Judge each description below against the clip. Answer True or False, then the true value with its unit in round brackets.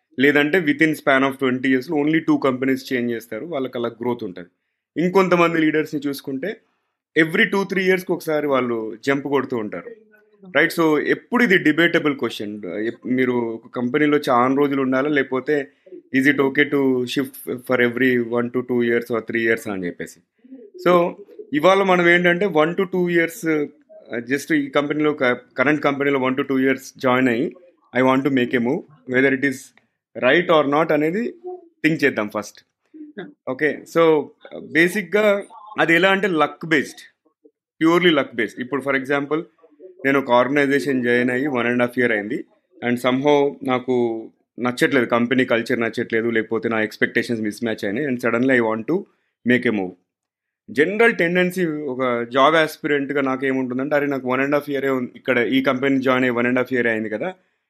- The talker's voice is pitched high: False (135 Hz)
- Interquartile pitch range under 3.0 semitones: False (4.5 semitones)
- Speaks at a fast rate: True (165 wpm)